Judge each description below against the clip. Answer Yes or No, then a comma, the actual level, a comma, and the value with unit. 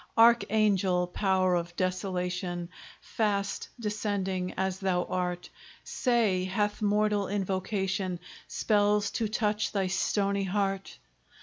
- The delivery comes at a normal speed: No, slow, 100 wpm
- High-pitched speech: Yes, high, 195 Hz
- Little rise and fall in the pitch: Yes, narrow, 2.1 semitones